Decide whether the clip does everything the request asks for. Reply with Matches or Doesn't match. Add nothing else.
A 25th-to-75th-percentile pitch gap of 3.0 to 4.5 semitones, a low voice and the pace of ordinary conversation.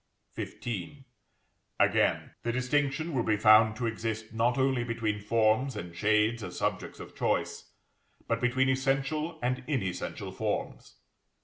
Doesn't match